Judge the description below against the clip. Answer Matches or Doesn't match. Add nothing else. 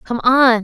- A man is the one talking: Doesn't match